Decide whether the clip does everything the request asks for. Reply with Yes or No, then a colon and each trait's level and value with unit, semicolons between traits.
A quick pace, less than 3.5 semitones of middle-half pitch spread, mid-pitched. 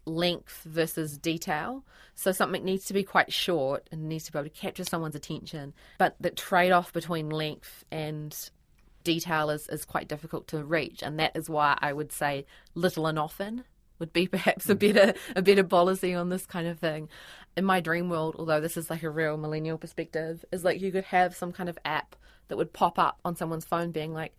Yes: fast, 210 wpm; narrow, 2.5 semitones; medium, 165 Hz